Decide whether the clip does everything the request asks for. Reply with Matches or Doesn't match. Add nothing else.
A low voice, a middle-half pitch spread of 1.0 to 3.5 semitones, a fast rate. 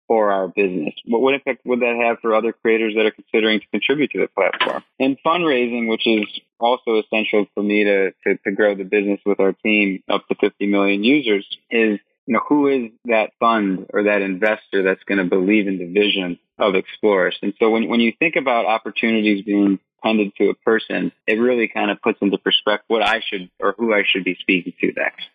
Matches